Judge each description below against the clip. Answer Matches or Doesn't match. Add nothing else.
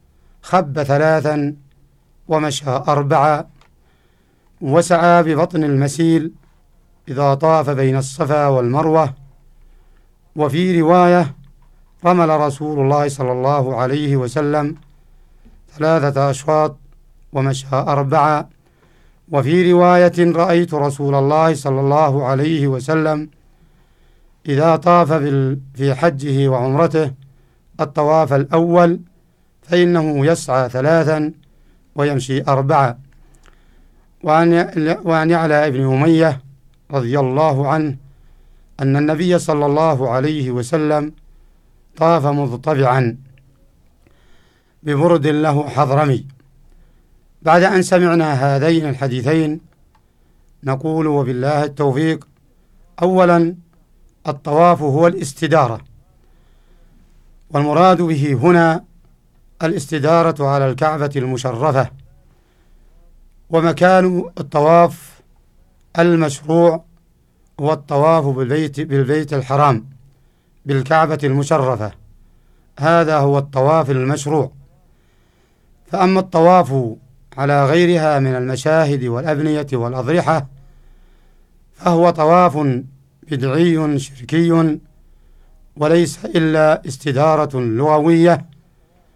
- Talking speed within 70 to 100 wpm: Matches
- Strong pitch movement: Doesn't match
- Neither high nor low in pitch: Matches